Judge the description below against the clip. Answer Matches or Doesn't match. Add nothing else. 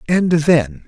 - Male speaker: Matches